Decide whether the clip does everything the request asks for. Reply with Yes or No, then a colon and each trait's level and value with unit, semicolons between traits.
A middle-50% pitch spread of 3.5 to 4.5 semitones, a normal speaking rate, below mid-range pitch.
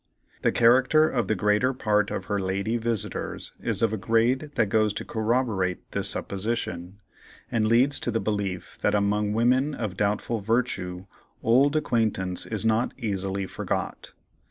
No: average, 2.9 semitones; average, 155 wpm; low, 110 Hz